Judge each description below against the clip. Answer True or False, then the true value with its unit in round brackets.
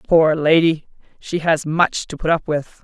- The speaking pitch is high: False (160 Hz)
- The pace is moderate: True (190 wpm)